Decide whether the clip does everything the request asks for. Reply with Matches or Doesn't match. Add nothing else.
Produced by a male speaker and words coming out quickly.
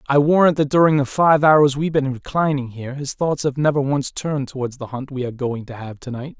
Matches